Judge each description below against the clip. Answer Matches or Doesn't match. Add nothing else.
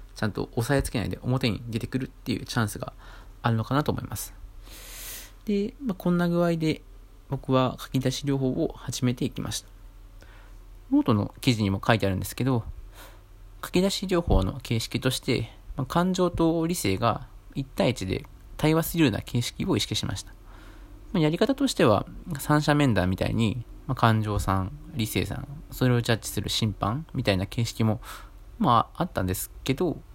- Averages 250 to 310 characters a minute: Doesn't match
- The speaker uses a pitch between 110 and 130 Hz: Matches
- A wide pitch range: Matches